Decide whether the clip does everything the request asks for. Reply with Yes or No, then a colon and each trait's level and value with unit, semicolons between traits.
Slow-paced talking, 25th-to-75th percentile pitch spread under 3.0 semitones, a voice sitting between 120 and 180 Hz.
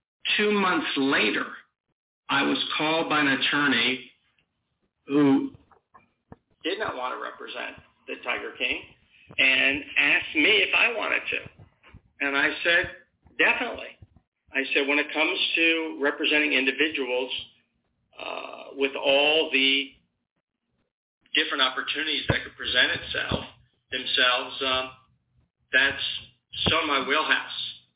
Yes: slow, 115 wpm; narrow, 2.4 semitones; medium, 140 Hz